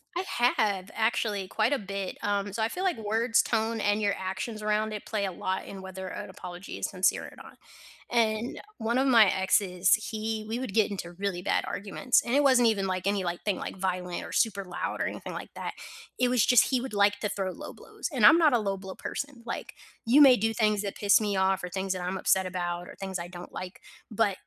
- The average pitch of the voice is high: Yes, high, 205 Hz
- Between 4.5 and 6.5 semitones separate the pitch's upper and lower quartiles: No, average, 3.0 semitones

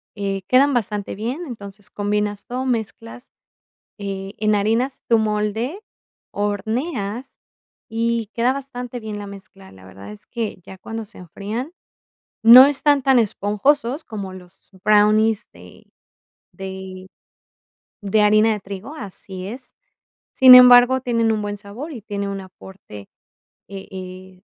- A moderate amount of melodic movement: Yes, average, 3.7 semitones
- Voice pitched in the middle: No, high, 215 Hz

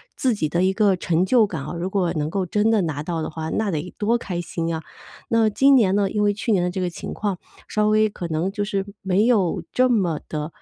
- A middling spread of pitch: Yes, average, 4.0 semitones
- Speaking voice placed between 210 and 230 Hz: No, high, 190 Hz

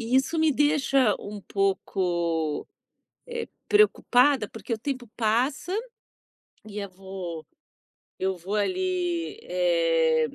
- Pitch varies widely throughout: Yes, wide, 8.0 semitones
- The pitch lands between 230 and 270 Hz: No, high, 210 Hz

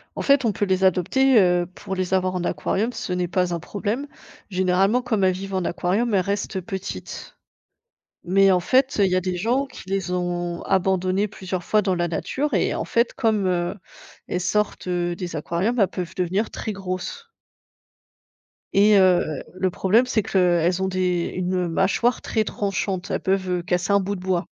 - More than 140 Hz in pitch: Yes, high, 190 Hz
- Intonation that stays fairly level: Yes, narrow, 2.3 semitones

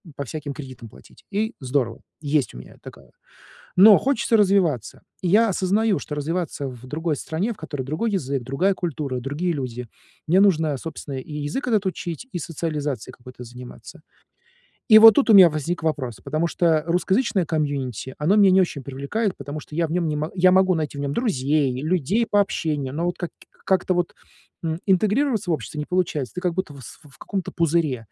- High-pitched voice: No, medium, 160 Hz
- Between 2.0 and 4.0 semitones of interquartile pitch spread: No, average, 5.0 semitones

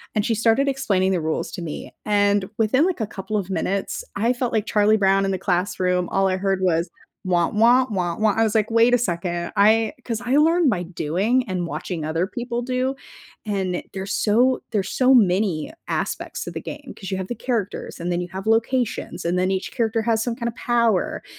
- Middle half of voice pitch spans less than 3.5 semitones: No, average, 4.1 semitones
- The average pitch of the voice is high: Yes, high, 205 Hz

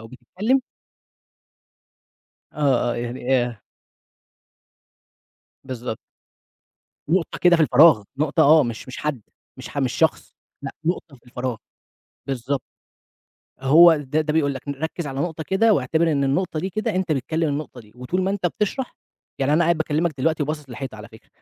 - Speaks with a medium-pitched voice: Yes, medium, 150 Hz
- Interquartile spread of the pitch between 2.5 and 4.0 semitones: No, average, 4.4 semitones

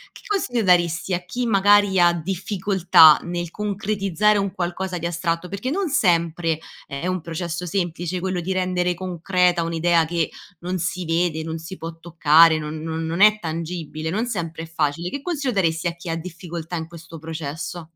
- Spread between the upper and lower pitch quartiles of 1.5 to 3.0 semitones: Yes, narrow, 2.5 semitones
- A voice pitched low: No, medium, 175 Hz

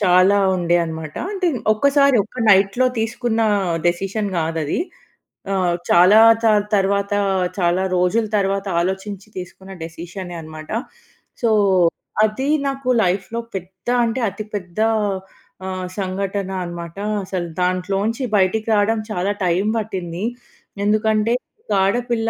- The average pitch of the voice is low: No, high, 195 Hz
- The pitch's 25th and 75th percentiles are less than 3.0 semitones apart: No, average, 3.3 semitones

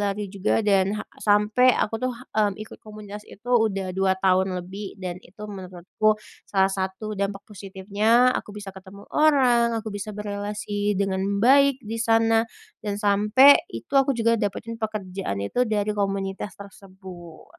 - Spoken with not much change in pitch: Yes, narrow, 2.2 semitones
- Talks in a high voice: Yes, high, 205 Hz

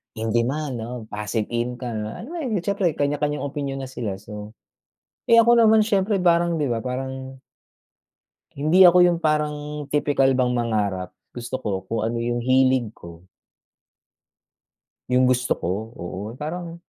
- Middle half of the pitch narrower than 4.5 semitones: No, average, 4.8 semitones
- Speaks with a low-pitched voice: Yes, low, 130 Hz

